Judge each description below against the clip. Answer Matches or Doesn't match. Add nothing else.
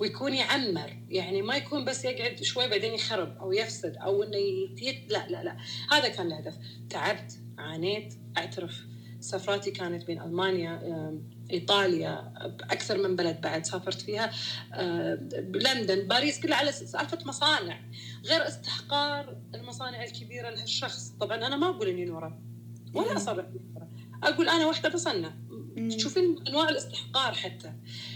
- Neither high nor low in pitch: Matches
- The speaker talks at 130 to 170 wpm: Matches